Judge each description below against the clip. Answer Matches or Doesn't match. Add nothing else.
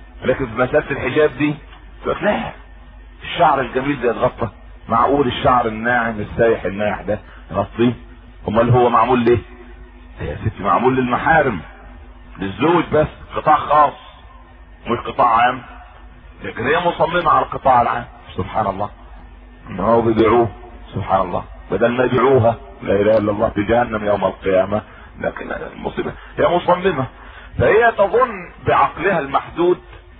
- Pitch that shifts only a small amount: Doesn't match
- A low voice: Matches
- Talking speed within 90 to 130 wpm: Matches